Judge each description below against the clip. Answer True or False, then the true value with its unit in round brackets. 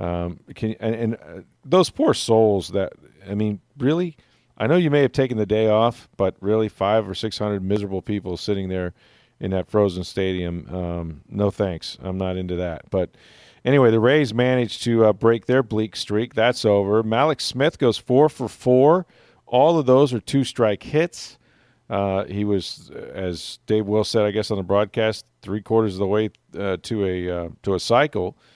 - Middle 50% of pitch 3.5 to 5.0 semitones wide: True (3.8 semitones)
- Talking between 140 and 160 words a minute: False (190 wpm)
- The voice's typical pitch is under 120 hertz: True (105 Hz)